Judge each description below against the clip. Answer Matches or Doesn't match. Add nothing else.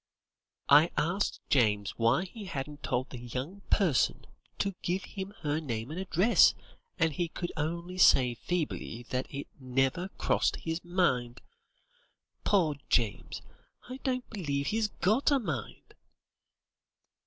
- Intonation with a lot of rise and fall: Matches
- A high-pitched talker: Doesn't match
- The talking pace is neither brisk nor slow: Doesn't match